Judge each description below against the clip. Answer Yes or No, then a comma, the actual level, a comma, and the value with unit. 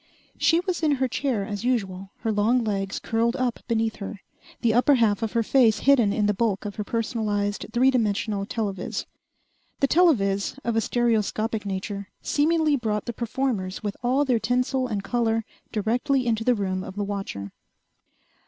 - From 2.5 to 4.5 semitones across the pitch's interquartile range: Yes, average, 3.5 semitones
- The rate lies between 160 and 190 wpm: Yes, average, 170 wpm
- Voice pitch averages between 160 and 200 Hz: No, high, 225 Hz